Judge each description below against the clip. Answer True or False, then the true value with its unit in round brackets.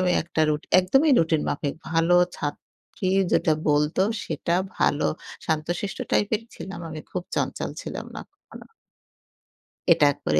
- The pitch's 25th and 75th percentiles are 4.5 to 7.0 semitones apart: False (3.5 semitones)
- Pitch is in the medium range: True (165 Hz)